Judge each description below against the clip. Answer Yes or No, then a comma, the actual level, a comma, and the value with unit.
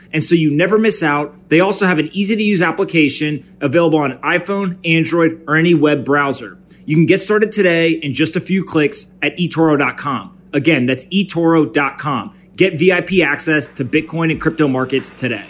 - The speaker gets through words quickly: No, average, 180 wpm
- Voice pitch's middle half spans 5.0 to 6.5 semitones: No, average, 3.6 semitones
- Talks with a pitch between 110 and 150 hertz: No, medium, 165 Hz